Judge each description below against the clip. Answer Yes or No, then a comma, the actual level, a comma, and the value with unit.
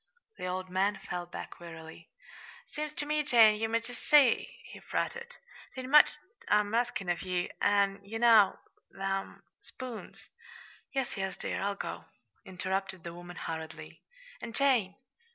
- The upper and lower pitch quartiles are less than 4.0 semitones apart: No, average, 5.1 semitones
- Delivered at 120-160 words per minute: Yes, average, 155 wpm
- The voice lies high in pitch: Yes, high, 200 Hz